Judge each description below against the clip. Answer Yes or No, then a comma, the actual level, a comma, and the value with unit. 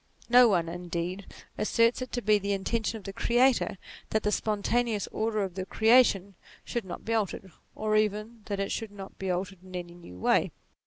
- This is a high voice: Yes, high, 205 Hz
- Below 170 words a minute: No, average, 195 wpm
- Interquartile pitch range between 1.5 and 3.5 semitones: Yes, average, 3.1 semitones